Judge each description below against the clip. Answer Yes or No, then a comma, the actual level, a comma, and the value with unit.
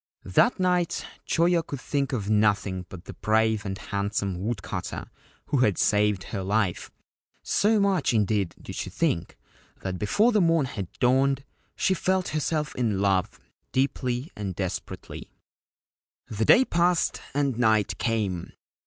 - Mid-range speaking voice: No, low, 110 Hz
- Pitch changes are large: Yes, wide, 7.2 semitones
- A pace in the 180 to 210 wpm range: No, average, 140 wpm